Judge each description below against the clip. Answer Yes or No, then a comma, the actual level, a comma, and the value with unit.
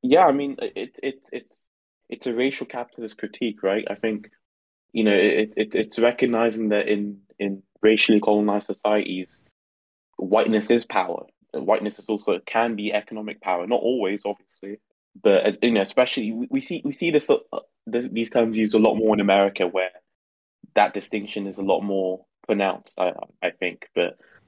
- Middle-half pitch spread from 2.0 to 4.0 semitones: Yes, average, 3.1 semitones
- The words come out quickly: No, average, 175 wpm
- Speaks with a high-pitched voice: No, low, 110 Hz